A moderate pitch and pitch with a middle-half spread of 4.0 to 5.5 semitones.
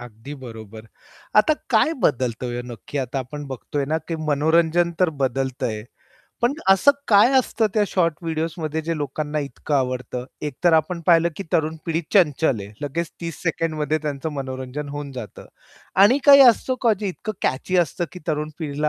Yes: medium, 150 Hz; average, 4.3 semitones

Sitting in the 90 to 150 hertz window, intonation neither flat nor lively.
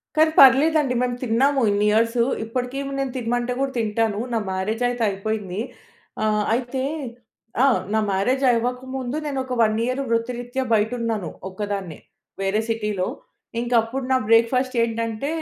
No: high, 230 Hz; average, 3.0 semitones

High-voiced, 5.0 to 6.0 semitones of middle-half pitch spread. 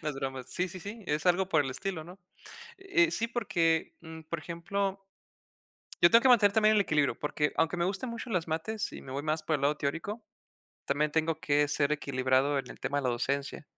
No: medium, 160 Hz; wide, 5.5 semitones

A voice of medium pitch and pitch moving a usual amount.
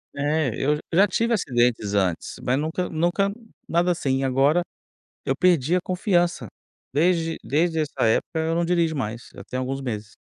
Yes: medium, 155 Hz; average, 4.9 semitones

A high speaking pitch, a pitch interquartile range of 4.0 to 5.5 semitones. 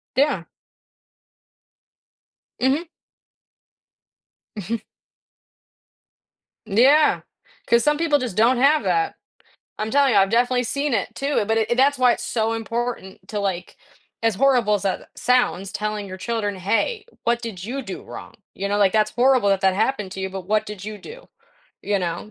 Yes: high, 225 Hz; average, 4.4 semitones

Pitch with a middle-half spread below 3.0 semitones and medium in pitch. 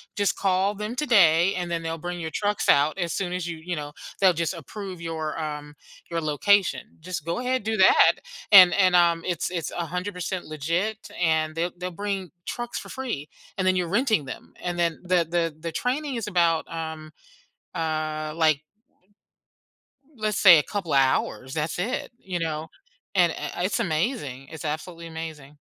No: average, 3.3 semitones; medium, 170 Hz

